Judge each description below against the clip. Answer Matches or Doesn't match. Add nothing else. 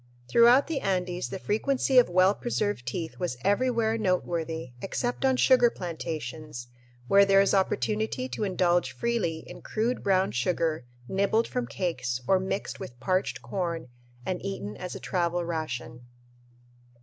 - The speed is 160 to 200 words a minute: Doesn't match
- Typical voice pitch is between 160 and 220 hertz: Matches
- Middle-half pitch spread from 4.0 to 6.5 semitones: Matches